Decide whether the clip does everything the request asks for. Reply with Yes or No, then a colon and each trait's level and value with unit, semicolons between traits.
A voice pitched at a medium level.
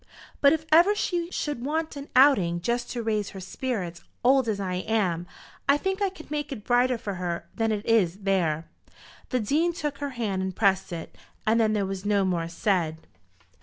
No: high, 220 Hz